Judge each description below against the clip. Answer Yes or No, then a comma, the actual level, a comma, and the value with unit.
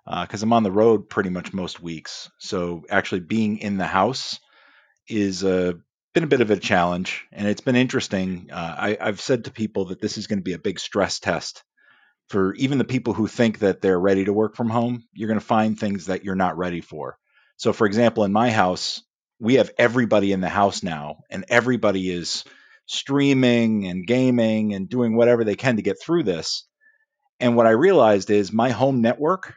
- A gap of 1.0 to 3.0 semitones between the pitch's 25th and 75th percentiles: No, average, 3.7 semitones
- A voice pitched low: Yes, low, 110 Hz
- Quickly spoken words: Yes, fast, 210 wpm